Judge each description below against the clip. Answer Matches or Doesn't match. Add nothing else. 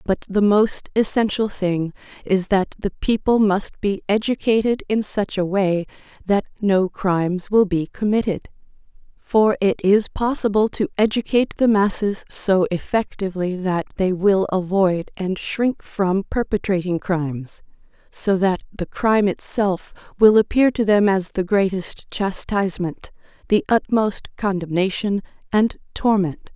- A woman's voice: Matches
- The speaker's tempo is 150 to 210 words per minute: Doesn't match